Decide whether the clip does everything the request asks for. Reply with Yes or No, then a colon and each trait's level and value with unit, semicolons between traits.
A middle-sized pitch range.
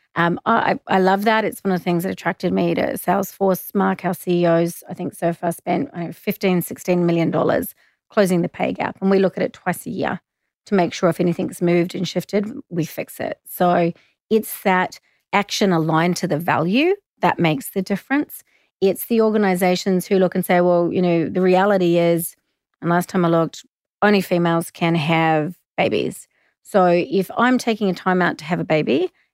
No: narrow, 2.3 semitones